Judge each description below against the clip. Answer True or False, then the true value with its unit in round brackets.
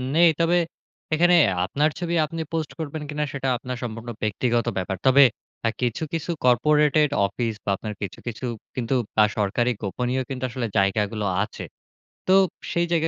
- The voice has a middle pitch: False (125 Hz)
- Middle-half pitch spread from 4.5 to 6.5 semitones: True (5.3 semitones)